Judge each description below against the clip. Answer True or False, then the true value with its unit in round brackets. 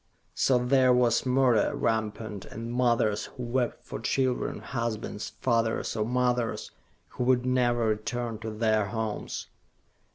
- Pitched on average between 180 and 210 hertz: False (120 Hz)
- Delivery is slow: True (130 wpm)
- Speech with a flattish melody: True (2.1 semitones)